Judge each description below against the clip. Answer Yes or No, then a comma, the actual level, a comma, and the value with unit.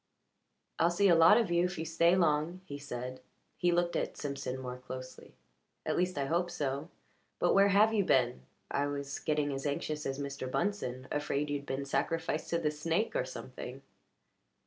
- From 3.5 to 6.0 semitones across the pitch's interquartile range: Yes, average, 3.9 semitones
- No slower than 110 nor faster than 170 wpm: No, average, 185 wpm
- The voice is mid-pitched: Yes, medium, 150 Hz